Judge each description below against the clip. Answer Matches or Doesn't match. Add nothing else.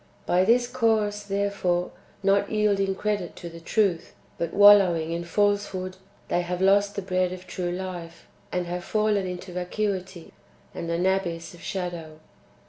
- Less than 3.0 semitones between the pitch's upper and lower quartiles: Matches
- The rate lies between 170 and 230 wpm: Doesn't match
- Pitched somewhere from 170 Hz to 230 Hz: Matches